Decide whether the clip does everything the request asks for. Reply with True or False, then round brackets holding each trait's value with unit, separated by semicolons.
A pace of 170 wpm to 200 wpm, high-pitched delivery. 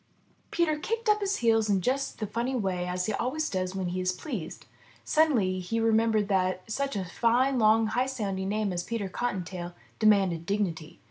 True (185 wpm; 215 Hz)